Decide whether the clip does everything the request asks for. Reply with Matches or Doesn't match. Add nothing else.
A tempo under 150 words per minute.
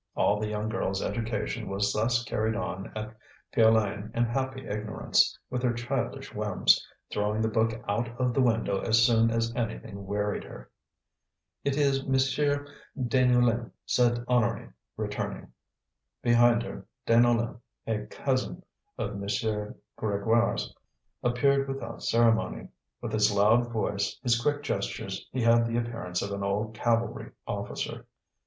Matches